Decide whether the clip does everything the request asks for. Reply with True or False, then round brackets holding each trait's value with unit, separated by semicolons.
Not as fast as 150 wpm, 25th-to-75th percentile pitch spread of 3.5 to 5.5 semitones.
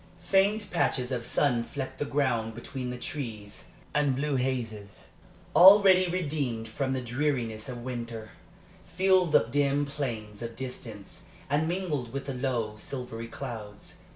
True (140 wpm; 4.0 semitones)